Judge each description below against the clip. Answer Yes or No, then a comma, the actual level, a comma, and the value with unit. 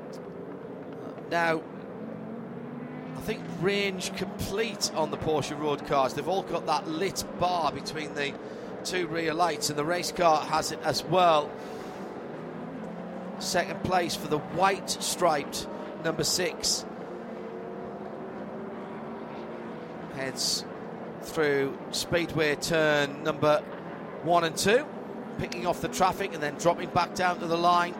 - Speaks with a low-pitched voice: No, medium, 170 Hz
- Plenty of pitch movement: No, average, 4.0 semitones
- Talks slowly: Yes, slow, 120 wpm